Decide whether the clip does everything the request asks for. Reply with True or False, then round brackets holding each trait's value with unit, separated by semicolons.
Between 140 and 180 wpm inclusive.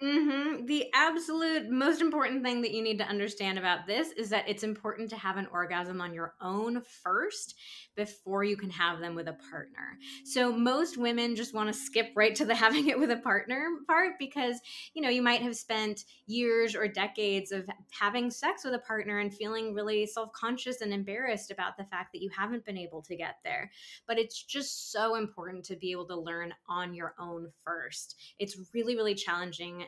False (200 wpm)